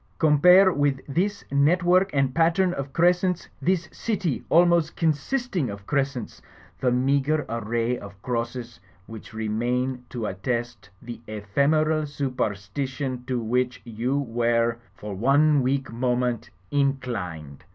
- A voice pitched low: Yes, low, 130 Hz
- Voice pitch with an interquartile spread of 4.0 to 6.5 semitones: Yes, average, 4.7 semitones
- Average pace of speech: No, slow, 120 wpm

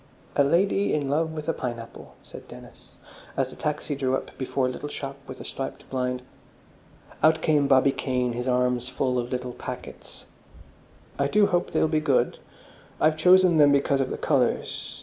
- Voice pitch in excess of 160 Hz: No, medium, 140 Hz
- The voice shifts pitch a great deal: No, average, 3.5 semitones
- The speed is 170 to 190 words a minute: Yes, average, 180 wpm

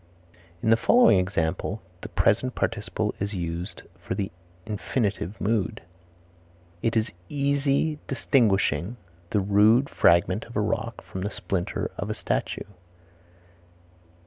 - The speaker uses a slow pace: Yes, slow, 120 wpm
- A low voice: Yes, low, 105 Hz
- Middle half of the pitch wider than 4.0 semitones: No, average, 3.6 semitones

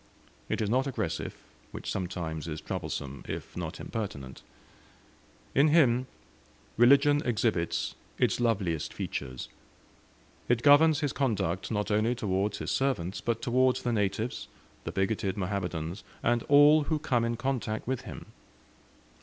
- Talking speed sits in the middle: No, slow, 130 wpm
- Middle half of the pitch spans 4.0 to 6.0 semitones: Yes, wide, 5.4 semitones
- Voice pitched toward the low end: Yes, low, 115 Hz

